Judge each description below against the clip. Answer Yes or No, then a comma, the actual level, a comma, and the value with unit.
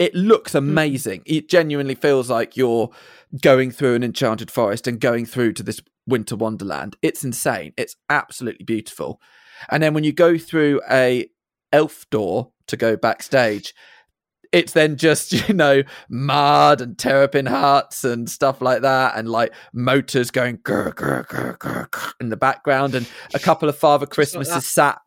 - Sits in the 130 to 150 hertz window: Yes, low, 135 Hz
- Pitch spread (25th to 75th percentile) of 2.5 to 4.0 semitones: Yes, average, 3.5 semitones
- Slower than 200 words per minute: Yes, average, 155 wpm